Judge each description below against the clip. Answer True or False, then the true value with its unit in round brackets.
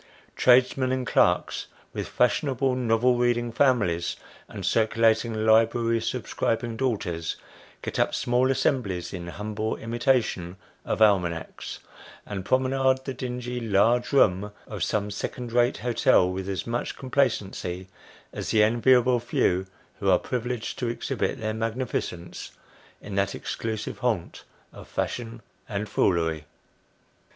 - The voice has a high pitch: False (115 Hz)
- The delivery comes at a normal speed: False (125 wpm)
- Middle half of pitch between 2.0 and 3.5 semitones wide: False (3.9 semitones)